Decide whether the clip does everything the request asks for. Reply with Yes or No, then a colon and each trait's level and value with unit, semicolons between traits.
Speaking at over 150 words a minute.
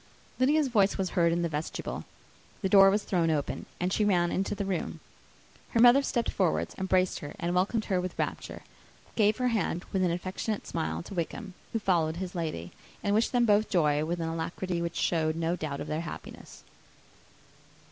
Yes: average, 190 wpm